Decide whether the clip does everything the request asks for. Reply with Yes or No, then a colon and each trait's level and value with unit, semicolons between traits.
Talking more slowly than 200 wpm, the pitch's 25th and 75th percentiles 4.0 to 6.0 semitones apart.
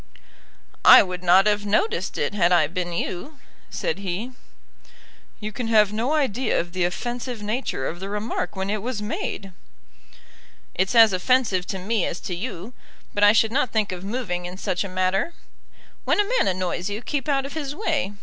Yes: average, 190 wpm; average, 4.9 semitones